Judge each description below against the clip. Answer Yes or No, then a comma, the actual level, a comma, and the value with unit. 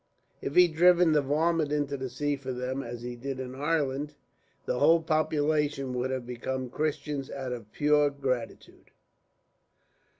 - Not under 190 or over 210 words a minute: No, average, 155 wpm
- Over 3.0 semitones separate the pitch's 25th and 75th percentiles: No, narrow, 2.6 semitones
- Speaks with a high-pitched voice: No, medium, 140 Hz